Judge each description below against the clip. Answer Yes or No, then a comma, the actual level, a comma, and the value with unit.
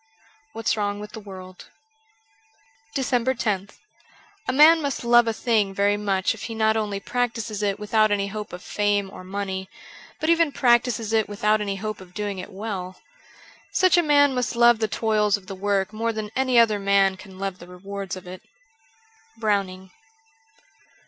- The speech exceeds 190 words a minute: No, average, 180 wpm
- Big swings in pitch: No, average, 3.0 semitones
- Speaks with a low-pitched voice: No, high, 210 Hz